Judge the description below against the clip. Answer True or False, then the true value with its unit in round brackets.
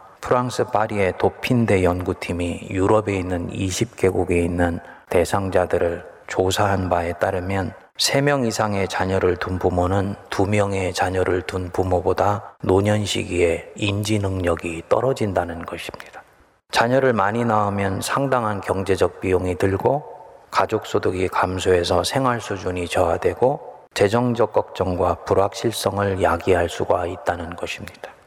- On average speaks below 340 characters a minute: True (290 characters per minute)